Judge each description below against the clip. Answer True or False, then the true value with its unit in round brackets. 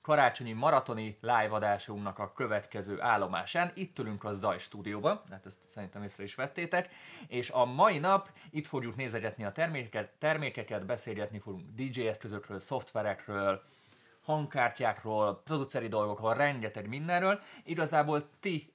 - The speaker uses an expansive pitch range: True (6.2 semitones)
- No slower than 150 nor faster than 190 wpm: False (130 wpm)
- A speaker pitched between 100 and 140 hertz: True (120 Hz)